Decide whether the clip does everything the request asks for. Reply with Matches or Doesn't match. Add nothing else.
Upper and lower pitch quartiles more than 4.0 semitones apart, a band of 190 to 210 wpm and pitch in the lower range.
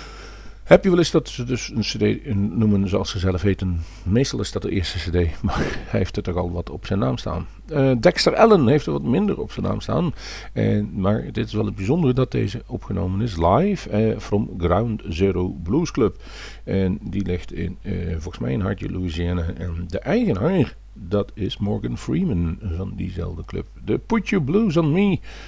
Matches